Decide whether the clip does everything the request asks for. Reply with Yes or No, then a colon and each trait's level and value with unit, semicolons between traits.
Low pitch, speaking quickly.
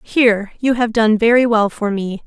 No: high, 225 Hz; fast, 210 wpm